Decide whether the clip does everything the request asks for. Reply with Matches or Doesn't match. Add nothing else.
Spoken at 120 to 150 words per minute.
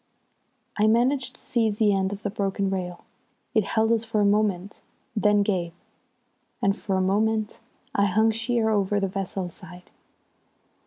Doesn't match